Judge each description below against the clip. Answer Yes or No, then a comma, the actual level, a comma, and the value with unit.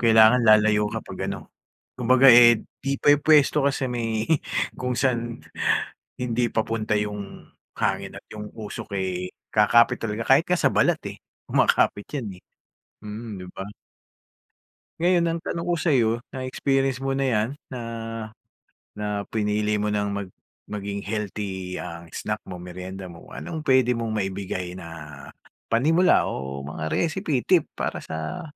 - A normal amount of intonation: Yes, average, 4.6 semitones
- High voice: No, low, 110 Hz